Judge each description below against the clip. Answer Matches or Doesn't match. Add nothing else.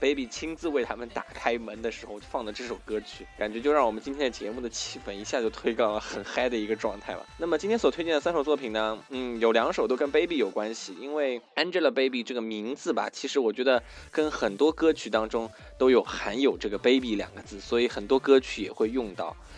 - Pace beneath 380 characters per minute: Doesn't match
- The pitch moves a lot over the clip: Doesn't match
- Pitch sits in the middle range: Doesn't match